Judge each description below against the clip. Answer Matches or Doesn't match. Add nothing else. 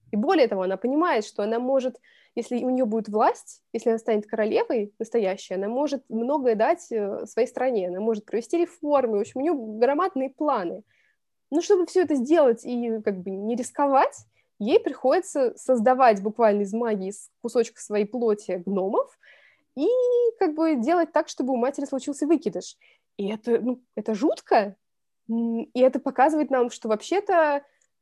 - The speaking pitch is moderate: Doesn't match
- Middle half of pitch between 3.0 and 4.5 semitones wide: Doesn't match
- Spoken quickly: Matches